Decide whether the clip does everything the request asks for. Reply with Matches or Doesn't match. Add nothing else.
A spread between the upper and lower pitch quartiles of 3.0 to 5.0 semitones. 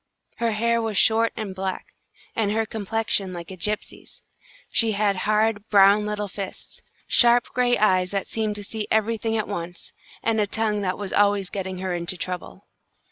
Doesn't match